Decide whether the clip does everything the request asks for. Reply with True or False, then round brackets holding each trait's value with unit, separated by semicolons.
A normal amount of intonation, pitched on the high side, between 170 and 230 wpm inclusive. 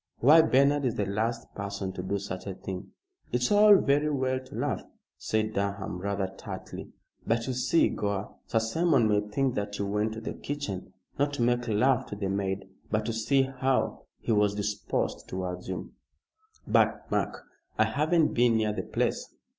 False (4.6 semitones; 110 Hz; 180 wpm)